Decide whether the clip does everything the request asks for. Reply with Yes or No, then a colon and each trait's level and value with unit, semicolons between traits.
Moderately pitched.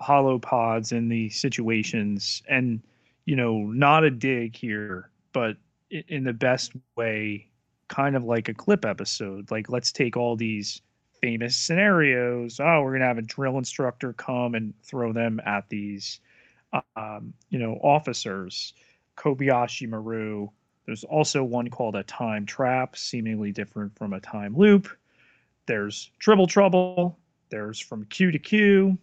No: low, 120 Hz